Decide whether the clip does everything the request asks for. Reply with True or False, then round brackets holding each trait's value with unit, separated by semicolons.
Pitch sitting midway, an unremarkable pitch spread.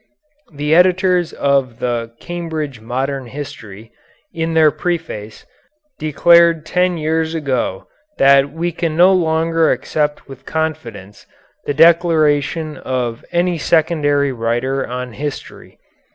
True (150 Hz; 3.9 semitones)